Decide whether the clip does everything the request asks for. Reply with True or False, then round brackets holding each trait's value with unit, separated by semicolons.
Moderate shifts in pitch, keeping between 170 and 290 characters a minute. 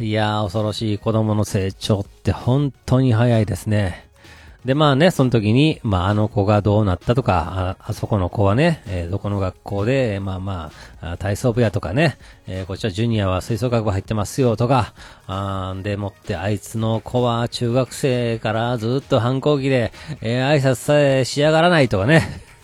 False (4.0 semitones; 340 characters per minute)